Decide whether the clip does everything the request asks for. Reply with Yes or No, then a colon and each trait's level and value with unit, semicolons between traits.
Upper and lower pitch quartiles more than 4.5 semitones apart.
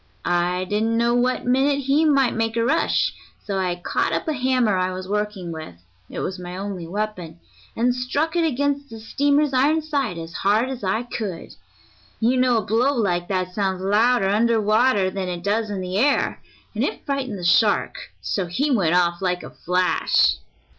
Yes: wide, 5.6 semitones